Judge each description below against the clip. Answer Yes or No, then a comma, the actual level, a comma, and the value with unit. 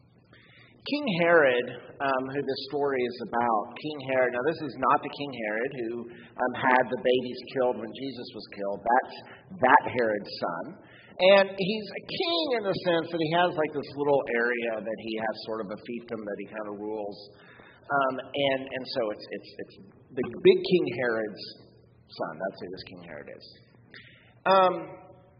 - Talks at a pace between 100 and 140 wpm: No, average, 180 wpm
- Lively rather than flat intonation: Yes, wide, 6.0 semitones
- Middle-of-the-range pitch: No, low, 130 Hz